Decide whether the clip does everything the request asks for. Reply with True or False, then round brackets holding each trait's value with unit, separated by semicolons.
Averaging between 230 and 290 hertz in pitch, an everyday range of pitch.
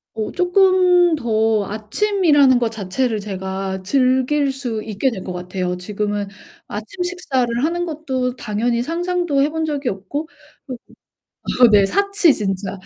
False (250 Hz; 7.5 semitones)